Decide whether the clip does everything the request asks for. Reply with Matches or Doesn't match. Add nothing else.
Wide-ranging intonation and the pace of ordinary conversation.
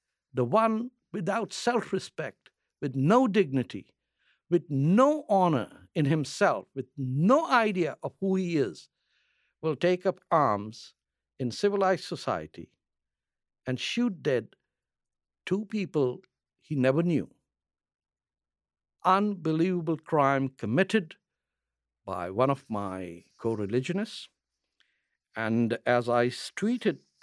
Doesn't match